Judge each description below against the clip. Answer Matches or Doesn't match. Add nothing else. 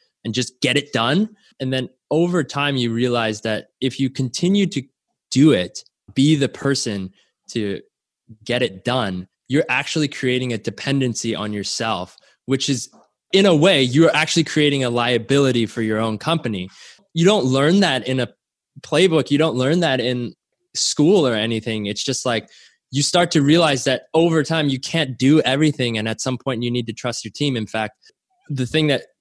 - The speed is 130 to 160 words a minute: Doesn't match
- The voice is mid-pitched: Doesn't match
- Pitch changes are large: Doesn't match